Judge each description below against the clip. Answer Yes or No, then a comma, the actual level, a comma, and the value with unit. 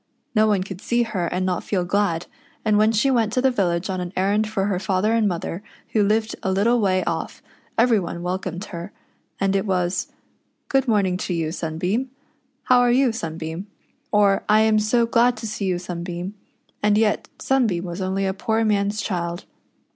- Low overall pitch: No, high, 200 Hz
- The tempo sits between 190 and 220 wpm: Yes, average, 200 wpm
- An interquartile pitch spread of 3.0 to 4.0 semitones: Yes, average, 3.4 semitones